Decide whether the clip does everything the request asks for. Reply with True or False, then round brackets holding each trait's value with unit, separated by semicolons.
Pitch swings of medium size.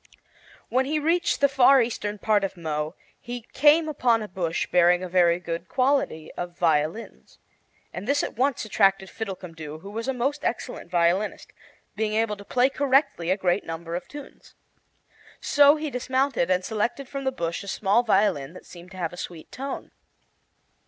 False (7.0 semitones)